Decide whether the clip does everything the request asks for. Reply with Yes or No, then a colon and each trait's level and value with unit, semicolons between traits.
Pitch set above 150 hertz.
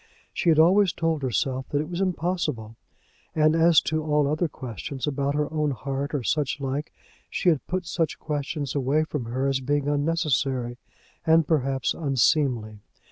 No: medium, 145 Hz